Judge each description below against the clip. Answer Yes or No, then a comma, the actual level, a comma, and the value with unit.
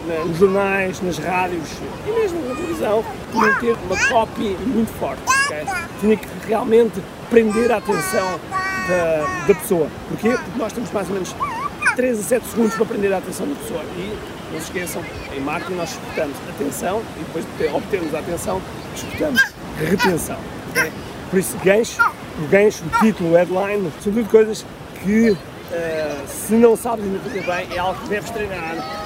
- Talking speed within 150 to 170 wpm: Yes, average, 165 wpm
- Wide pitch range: No, average, 3.9 semitones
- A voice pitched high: Yes, high, 205 Hz